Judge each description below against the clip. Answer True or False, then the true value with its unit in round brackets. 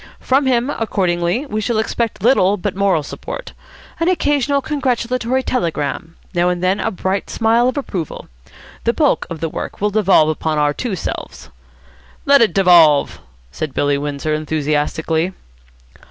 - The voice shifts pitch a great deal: True (7.4 semitones)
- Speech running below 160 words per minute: True (150 wpm)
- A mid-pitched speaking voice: False (195 Hz)